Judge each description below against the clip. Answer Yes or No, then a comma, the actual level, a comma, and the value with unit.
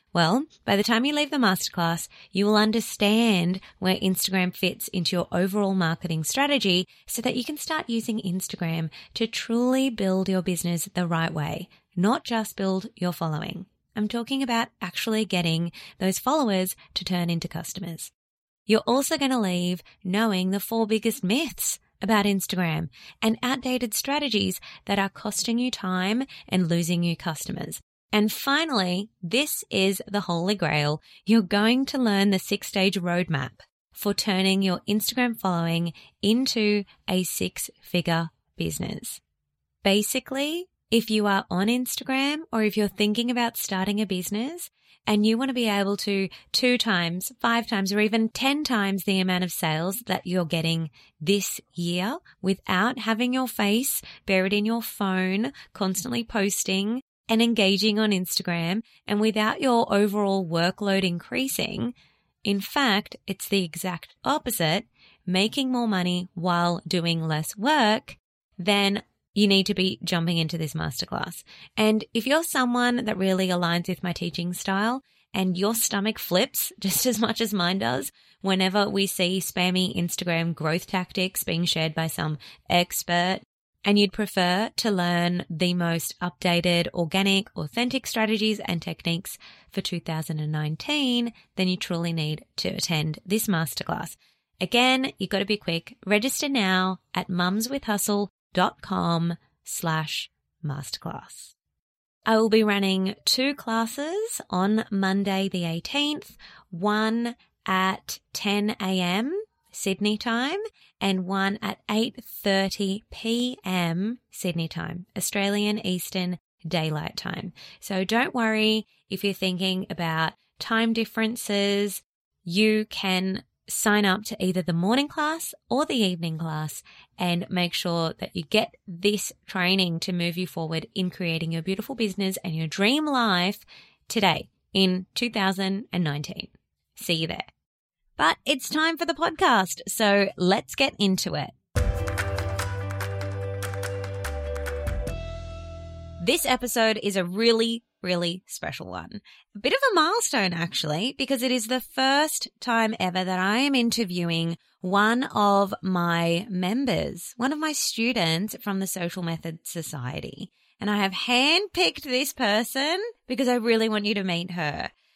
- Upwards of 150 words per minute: No, average, 140 wpm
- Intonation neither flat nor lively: Yes, average, 4.4 semitones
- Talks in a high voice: Yes, high, 195 Hz